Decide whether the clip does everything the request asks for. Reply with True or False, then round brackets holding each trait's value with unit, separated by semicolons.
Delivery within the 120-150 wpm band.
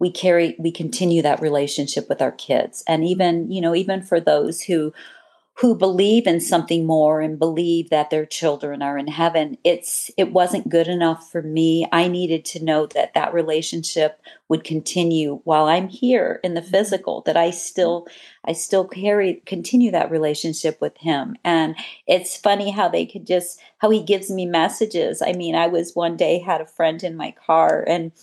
False (185 wpm)